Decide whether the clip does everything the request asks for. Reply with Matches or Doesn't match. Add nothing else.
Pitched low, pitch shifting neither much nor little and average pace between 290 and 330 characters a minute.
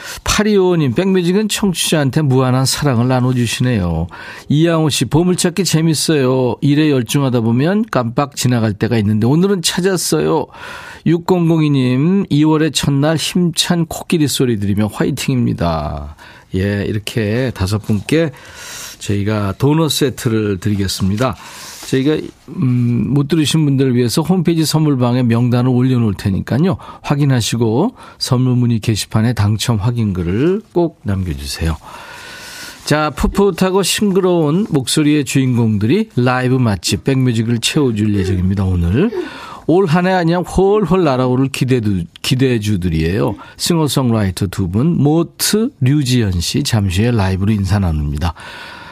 Doesn't match